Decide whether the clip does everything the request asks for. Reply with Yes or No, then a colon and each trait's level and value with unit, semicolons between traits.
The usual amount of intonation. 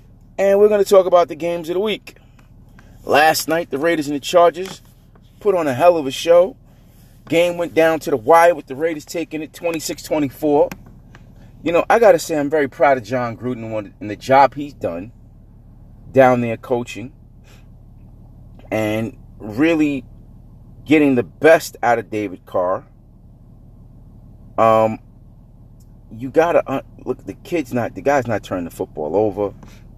No: wide, 5.8 semitones